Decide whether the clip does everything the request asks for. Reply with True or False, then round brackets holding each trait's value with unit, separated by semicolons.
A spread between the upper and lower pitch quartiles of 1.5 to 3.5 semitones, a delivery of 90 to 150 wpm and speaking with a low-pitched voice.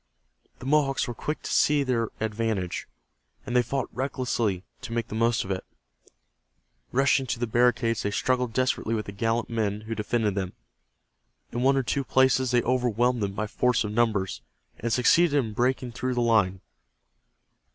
False (2.9 semitones; 170 wpm; 120 Hz)